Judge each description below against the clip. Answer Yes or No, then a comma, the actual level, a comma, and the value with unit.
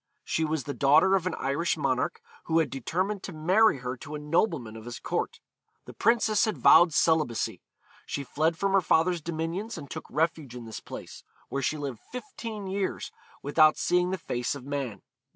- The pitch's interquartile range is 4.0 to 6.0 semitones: Yes, average, 5.1 semitones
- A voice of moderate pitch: Yes, medium, 160 Hz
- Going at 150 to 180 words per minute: No, average, 190 wpm